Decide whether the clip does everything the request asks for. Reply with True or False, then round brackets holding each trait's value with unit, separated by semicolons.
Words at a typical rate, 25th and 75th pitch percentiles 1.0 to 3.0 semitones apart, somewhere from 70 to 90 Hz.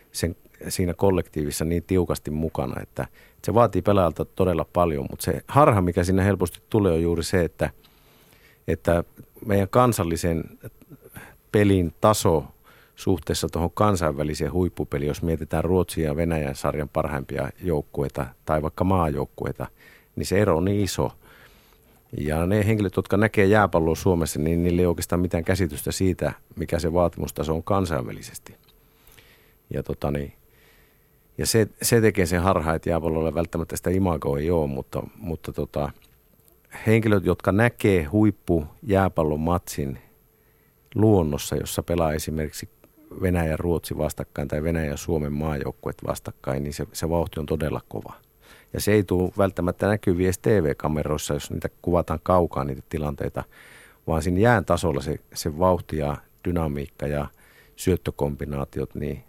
False (140 wpm; 3.8 semitones; 85 Hz)